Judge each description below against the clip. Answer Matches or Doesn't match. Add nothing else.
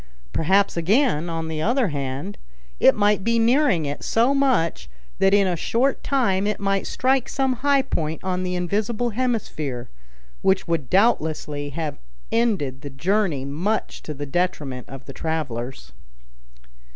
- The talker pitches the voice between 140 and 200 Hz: Matches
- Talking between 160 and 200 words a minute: Doesn't match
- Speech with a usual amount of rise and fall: Doesn't match